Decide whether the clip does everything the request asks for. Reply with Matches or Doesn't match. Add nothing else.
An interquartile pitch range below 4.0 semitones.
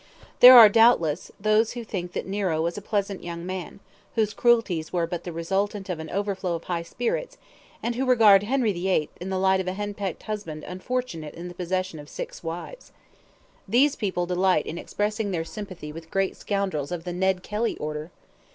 Matches